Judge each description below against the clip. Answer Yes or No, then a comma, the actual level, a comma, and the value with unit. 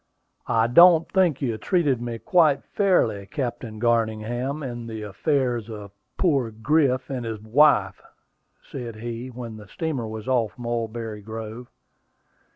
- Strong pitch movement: No, average, 3.9 semitones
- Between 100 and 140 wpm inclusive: Yes, slow, 135 wpm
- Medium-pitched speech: No, low, 120 Hz